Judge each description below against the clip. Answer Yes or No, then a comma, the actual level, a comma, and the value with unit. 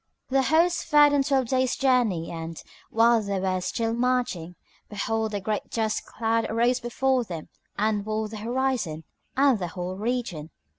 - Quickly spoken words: No, average, 160 wpm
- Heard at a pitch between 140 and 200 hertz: No, high, 225 Hz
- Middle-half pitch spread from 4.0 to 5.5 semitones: Yes, average, 4.5 semitones